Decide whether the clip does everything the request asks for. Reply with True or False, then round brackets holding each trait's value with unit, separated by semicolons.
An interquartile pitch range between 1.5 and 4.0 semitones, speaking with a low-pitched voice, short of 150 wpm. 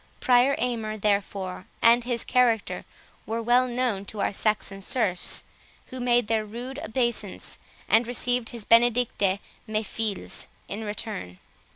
False (2.8 semitones; 225 Hz; 135 wpm)